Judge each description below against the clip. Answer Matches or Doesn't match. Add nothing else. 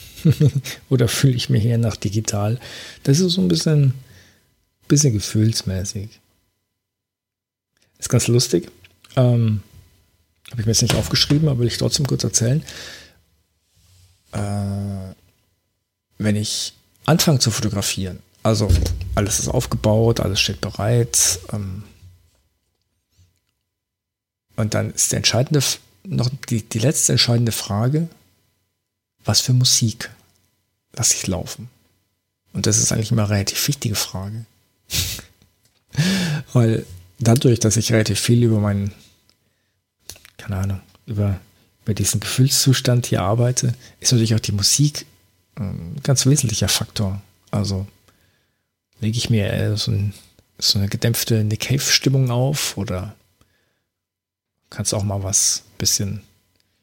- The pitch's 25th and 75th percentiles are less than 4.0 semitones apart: Matches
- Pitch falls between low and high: Doesn't match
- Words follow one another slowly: Matches